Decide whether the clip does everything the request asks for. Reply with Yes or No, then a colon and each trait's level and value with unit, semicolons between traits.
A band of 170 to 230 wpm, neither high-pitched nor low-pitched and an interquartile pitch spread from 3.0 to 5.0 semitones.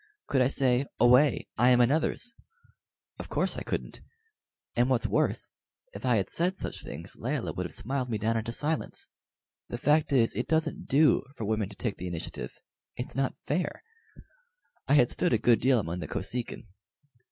No: average, 180 wpm; low, 125 Hz; average, 3.7 semitones